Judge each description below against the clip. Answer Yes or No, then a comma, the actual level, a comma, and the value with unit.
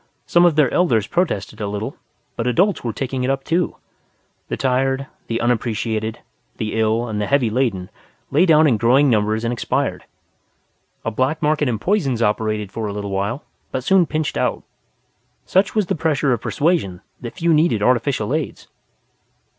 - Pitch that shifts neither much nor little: No, wide, 5.7 semitones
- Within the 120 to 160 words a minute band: No, average, 170 wpm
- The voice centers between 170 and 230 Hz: No, low, 125 Hz